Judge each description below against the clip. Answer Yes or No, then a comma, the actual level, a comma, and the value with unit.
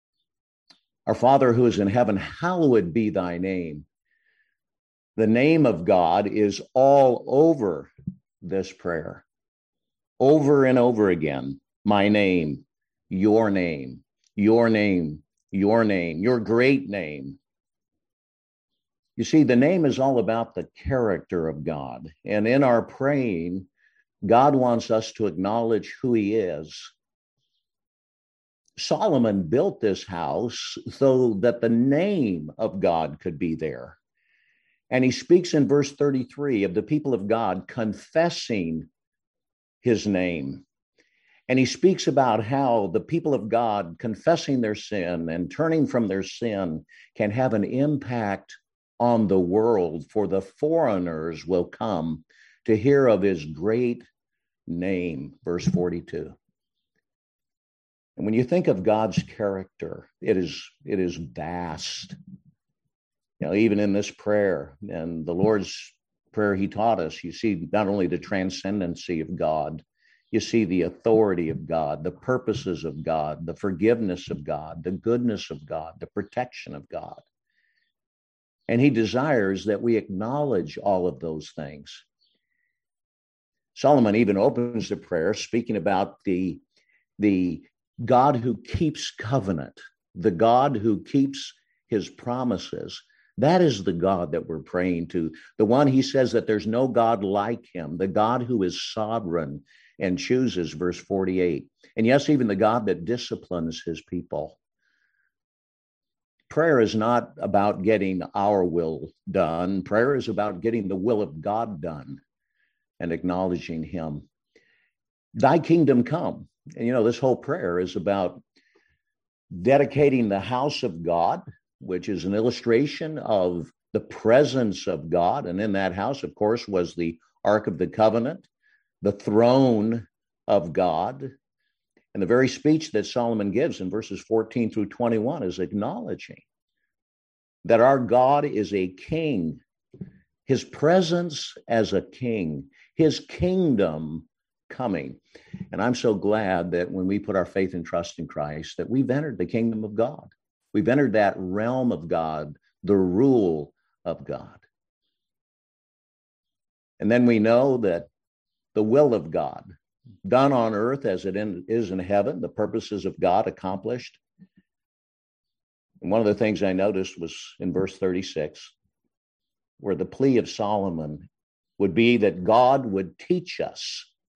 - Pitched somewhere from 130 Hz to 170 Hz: No, low, 105 Hz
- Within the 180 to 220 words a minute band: No, average, 140 wpm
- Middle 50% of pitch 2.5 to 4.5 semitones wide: No, wide, 5.5 semitones